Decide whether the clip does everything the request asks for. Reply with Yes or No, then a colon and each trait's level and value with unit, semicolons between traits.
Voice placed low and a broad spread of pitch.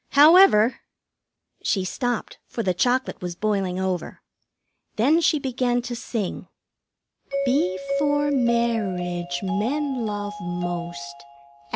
No: high, 220 Hz; wide, 6.4 semitones